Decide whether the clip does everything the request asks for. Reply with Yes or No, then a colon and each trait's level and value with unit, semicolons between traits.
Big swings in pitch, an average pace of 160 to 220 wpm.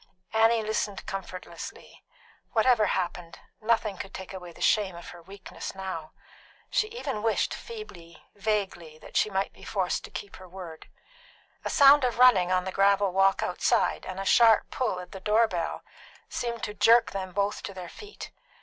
No: average, 3.3 semitones; average, 175 wpm